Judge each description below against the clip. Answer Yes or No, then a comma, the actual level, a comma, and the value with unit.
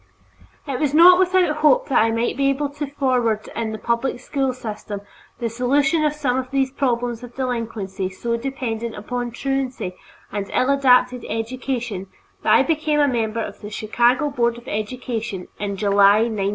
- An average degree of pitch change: Yes, average, 3.7 semitones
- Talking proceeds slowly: No, average, 175 wpm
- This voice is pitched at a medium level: No, high, 245 Hz